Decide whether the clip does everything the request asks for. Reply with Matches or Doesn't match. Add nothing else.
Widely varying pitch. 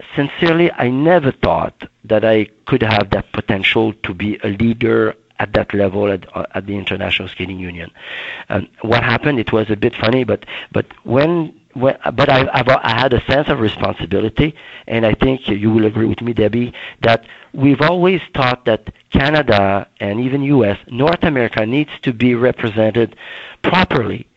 Doesn't match